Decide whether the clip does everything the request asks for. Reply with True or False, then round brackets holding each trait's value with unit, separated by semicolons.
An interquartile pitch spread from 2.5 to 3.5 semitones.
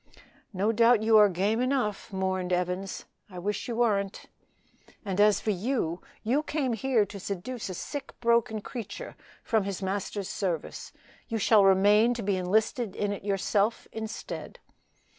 True (3.1 semitones)